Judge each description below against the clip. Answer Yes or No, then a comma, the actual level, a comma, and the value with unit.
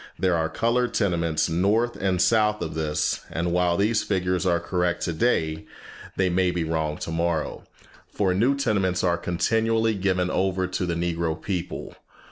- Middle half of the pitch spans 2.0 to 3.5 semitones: Yes, average, 3.2 semitones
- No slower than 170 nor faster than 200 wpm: No, average, 155 wpm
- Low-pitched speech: Yes, very low, 90 Hz